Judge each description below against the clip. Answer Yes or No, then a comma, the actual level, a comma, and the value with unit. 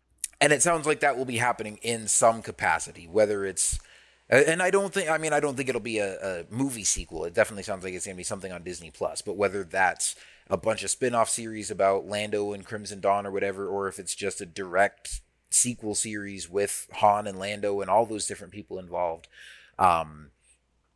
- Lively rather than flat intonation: No, average, 3.0 semitones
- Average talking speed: No, fast, 215 wpm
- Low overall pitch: Yes, low, 105 Hz